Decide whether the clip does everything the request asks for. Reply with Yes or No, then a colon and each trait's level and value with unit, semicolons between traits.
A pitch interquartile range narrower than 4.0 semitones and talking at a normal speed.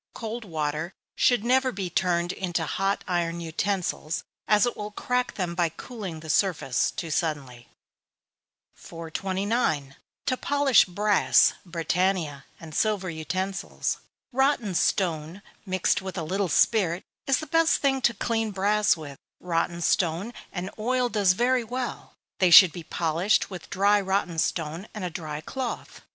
No: average, 4.4 semitones; average, 145 wpm